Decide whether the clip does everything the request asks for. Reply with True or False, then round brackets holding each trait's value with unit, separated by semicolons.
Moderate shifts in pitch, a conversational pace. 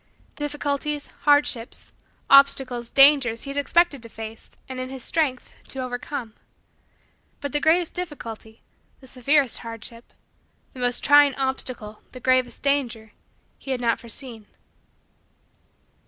False (3.3 semitones; 125 wpm)